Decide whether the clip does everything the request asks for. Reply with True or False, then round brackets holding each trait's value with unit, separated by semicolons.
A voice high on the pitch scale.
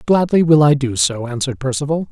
False (145 Hz)